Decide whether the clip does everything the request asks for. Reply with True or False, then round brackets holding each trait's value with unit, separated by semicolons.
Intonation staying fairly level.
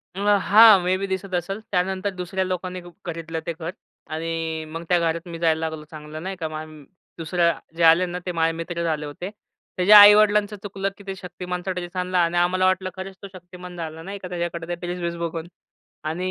True (2.2 semitones)